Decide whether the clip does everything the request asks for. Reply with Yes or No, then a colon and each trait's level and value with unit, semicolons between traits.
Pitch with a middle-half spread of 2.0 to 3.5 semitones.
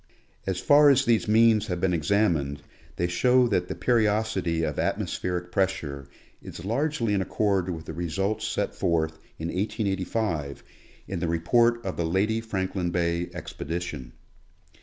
No: average, 4.5 semitones